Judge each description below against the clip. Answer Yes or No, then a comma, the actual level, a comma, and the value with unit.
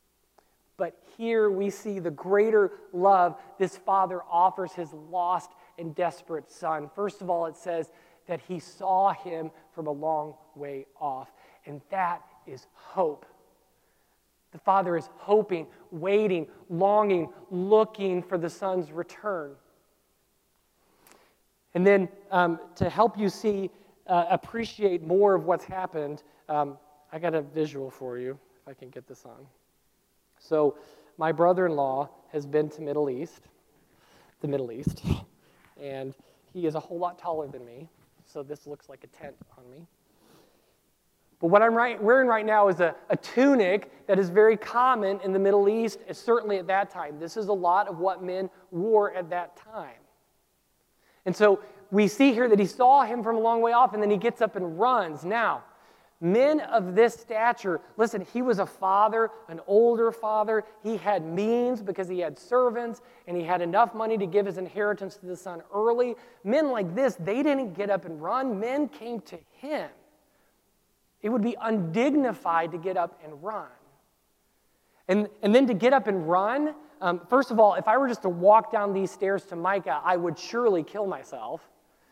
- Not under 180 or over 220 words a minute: No, average, 170 wpm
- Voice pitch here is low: No, high, 190 Hz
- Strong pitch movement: No, average, 4.3 semitones